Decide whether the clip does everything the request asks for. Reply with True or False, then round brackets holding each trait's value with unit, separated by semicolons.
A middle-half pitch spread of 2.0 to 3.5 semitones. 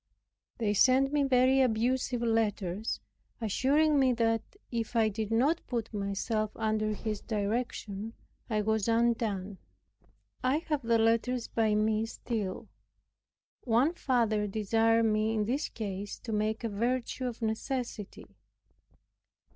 True (2.6 semitones)